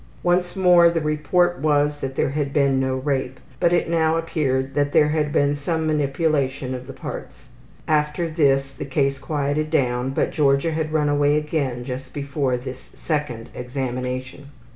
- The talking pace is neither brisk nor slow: Yes, average, 165 wpm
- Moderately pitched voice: Yes, medium, 145 Hz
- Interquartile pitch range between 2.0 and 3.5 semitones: Yes, average, 2.7 semitones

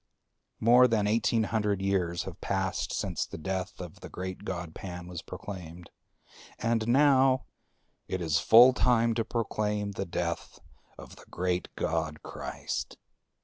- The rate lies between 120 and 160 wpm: Yes, average, 145 wpm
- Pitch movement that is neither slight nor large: Yes, average, 4.5 semitones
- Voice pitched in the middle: No, very low, 95 Hz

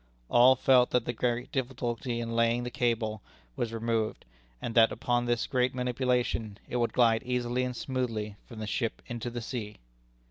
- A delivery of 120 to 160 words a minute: No, average, 175 wpm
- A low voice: Yes, low, 120 Hz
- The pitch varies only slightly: Yes, narrow, 1.5 semitones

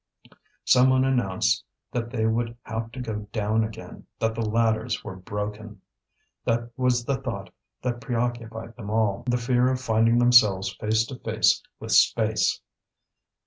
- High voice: No, low, 115 Hz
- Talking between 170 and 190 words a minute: No, average, 145 wpm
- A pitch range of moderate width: No, narrow, 2.0 semitones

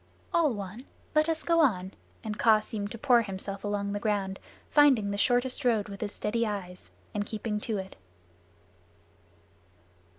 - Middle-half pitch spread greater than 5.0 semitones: No, average, 3.3 semitones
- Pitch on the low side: No, high, 210 Hz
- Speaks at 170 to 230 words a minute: No, average, 160 wpm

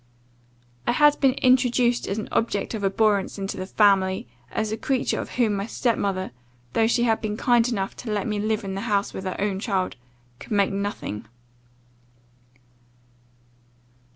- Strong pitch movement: No, average, 3.1 semitones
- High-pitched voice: Yes, high, 210 Hz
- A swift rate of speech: No, average, 170 wpm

